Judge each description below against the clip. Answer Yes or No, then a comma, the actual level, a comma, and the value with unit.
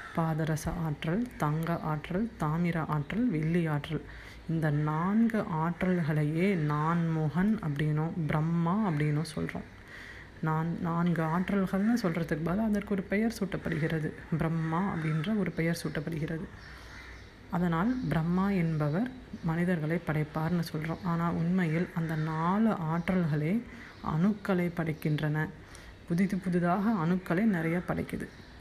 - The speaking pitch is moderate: Yes, medium, 165 Hz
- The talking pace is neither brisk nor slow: Yes, average, 105 wpm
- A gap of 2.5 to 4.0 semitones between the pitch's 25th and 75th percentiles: Yes, average, 2.8 semitones